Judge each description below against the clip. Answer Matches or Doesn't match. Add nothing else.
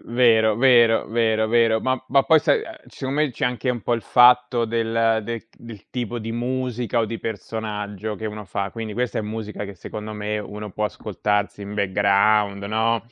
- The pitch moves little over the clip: Matches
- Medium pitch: Doesn't match